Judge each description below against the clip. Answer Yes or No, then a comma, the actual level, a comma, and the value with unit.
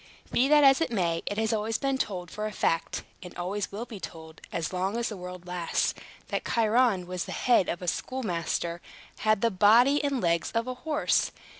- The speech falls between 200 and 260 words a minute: Yes, fast, 205 wpm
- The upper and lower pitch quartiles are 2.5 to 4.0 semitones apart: No, average, 5.1 semitones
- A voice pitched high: Yes, high, 210 Hz